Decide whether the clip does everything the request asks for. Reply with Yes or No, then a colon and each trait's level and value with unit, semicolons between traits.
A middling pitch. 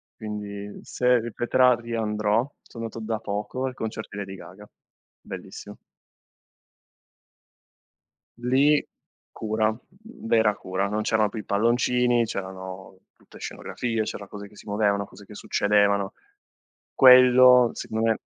No: low, 110 Hz